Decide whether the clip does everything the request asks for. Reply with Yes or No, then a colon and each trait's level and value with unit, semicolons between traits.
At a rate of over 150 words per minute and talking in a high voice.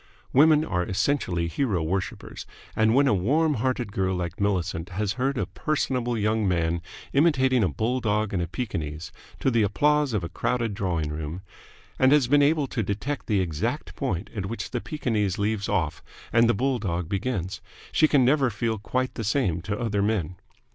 No: average, 180 wpm; low, 105 Hz